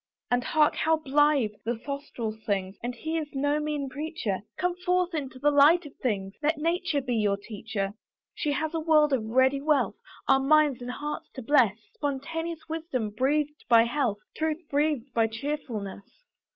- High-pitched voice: Yes, very high, 280 Hz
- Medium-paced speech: Yes, average, 170 wpm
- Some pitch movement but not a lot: Yes, average, 4.6 semitones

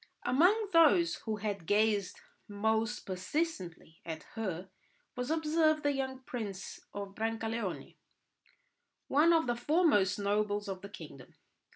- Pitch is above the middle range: Yes, high, 220 Hz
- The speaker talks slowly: Yes, slow, 125 wpm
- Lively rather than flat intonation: Yes, wide, 6.9 semitones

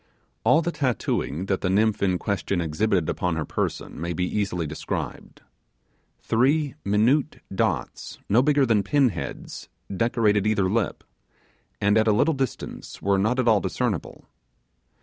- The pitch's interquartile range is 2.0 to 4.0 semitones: No, average, 4.8 semitones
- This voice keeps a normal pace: Yes, average, 150 wpm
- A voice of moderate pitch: No, low, 105 Hz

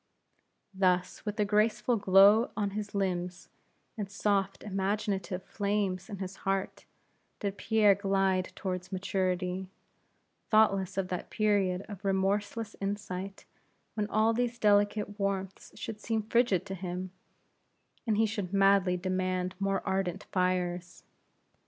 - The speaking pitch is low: No, high, 195 Hz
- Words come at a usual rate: No, slow, 125 wpm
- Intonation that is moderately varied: No, narrow, 2.0 semitones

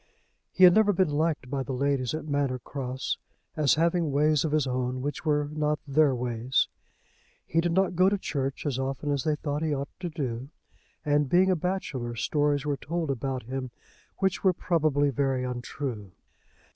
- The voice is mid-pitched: Yes, medium, 145 Hz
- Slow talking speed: No, average, 185 wpm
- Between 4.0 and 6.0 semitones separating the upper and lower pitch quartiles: No, average, 3.3 semitones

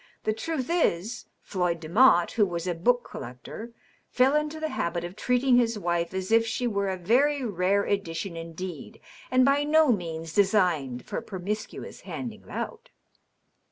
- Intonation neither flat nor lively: No, wide, 6.3 semitones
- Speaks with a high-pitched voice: Yes, high, 205 Hz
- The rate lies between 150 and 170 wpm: Yes, average, 160 wpm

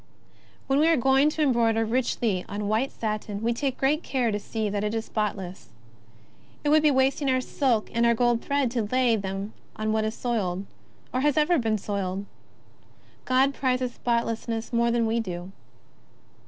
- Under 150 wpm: No, average, 175 wpm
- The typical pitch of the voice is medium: No, high, 235 Hz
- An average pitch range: Yes, average, 3.6 semitones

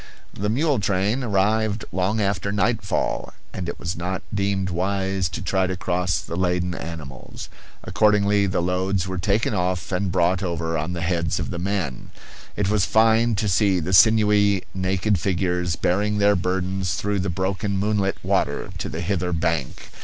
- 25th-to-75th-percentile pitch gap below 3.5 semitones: Yes, narrow, 2.4 semitones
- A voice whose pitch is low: Yes, very low, 95 Hz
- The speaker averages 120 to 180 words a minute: Yes, average, 170 wpm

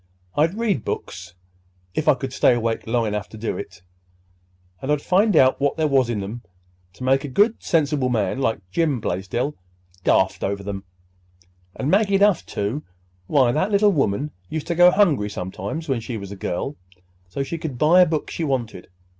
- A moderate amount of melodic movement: No, wide, 8.5 semitones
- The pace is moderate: Yes, average, 180 wpm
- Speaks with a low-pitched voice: Yes, low, 120 Hz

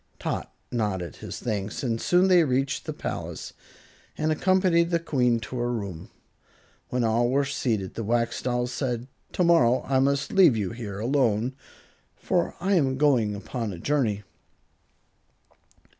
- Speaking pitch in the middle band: No, low, 125 Hz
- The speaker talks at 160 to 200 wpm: No, average, 145 wpm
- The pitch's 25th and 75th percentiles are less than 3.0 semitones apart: No, average, 4.5 semitones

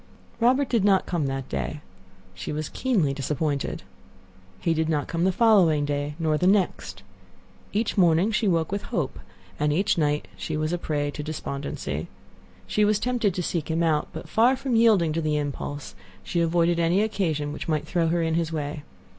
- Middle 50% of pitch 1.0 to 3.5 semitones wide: No, average, 4.7 semitones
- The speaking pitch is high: No, medium, 165 Hz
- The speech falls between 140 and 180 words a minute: No, average, 190 wpm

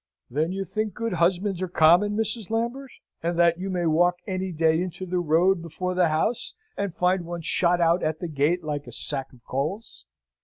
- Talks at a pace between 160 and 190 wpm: No, average, 200 wpm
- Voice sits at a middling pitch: Yes, medium, 175 Hz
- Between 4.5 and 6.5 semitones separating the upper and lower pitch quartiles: No, average, 2.8 semitones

